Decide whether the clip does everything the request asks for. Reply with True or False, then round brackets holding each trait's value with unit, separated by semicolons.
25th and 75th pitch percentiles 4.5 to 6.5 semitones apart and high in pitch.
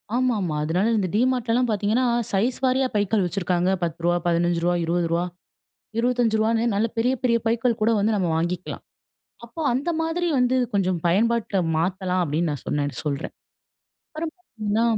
True (5.6 semitones; 210 Hz)